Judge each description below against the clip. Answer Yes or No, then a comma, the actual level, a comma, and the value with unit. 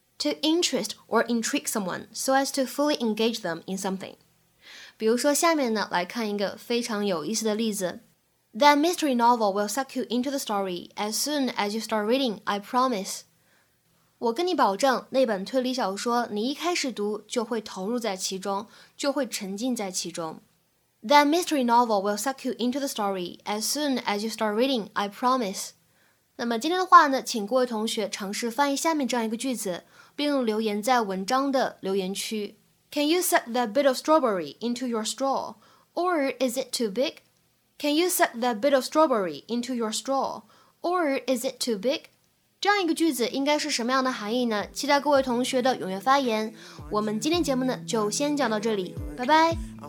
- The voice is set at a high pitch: Yes, high, 240 Hz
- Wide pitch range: No, average, 4.5 semitones